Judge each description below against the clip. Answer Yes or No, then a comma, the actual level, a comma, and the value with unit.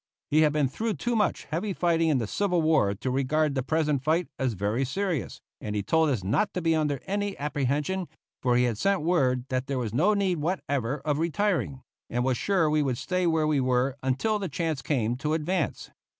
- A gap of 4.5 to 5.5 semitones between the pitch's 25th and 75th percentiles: Yes, average, 5.1 semitones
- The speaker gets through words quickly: Yes, fast, 215 wpm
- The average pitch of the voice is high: No, medium, 150 Hz